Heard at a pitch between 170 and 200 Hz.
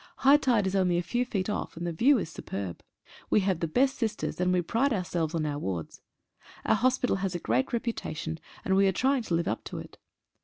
Yes: high, 190 Hz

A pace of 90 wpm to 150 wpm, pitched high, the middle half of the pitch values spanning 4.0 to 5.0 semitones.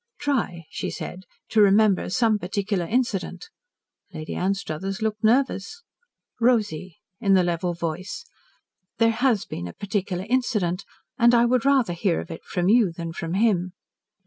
Yes: average, 145 wpm; high, 200 Hz; average, 4.4 semitones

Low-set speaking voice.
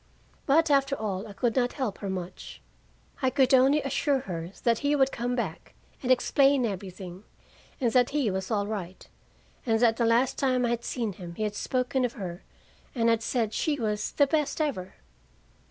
No: high, 235 Hz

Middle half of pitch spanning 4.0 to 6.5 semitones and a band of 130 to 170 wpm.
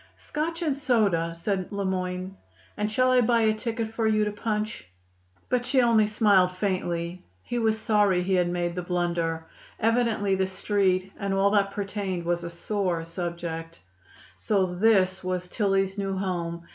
No: average, 3.4 semitones; average, 165 wpm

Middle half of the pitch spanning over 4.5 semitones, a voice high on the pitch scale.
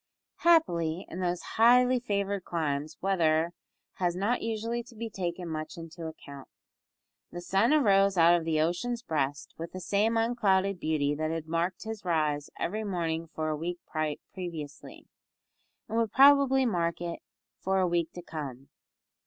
No: average, 5.0 semitones; medium, 175 Hz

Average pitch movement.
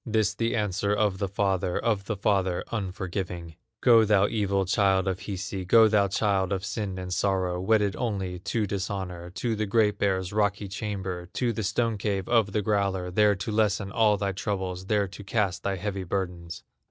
No: narrow, 2.0 semitones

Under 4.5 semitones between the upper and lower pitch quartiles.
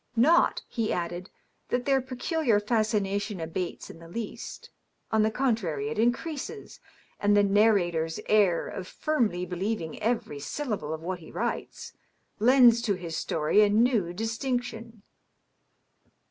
No: average, 5.2 semitones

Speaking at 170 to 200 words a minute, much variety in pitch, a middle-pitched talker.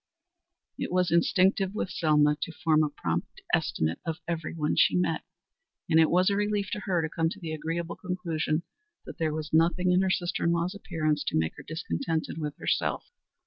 No: average, 195 wpm; narrow, 2.5 semitones; medium, 165 Hz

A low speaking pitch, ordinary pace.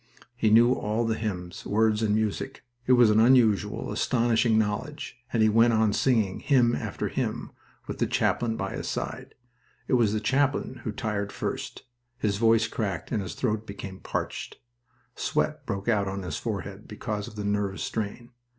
Yes: low, 110 Hz; average, 175 wpm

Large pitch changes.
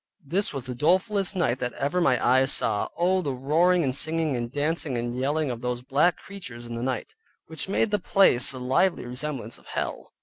Yes: wide, 5.9 semitones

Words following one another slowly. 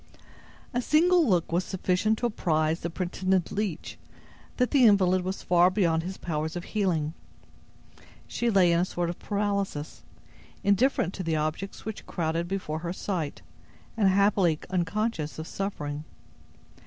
No: average, 145 wpm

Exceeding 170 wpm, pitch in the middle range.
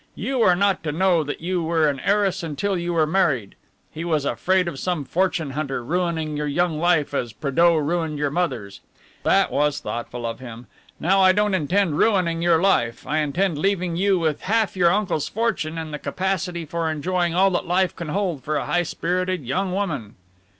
Yes: average, 195 wpm; medium, 170 Hz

